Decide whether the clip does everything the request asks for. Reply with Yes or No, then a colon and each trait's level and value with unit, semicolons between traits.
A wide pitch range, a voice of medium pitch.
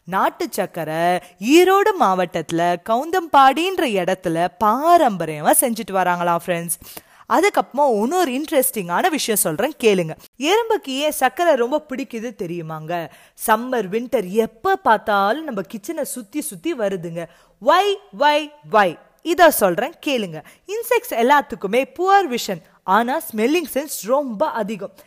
No: wide, 8.0 semitones; high, 235 Hz